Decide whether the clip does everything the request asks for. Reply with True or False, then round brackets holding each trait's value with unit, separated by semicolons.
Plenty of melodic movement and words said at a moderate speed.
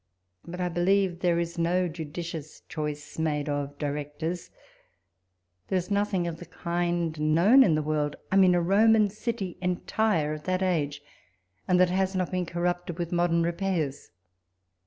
False (2.9 semitones; 155 wpm)